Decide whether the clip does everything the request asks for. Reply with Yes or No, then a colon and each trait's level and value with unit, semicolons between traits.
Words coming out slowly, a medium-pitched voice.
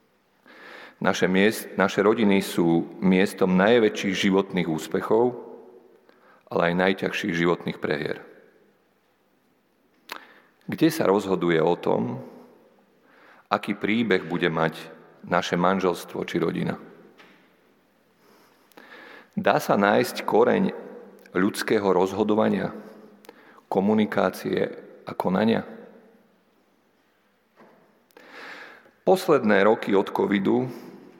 No: slow, 75 wpm; very low, 95 Hz